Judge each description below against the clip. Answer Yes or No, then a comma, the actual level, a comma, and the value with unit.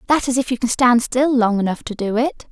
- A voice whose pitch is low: No, high, 245 Hz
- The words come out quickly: Yes, fast, 285 wpm